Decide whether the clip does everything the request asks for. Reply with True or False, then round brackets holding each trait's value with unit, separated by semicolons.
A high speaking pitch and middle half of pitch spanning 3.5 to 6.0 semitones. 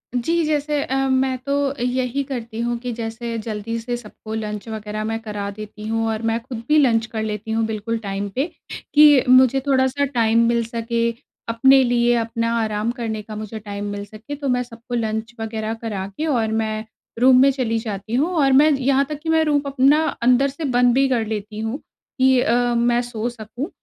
False (235 Hz; 3.1 semitones)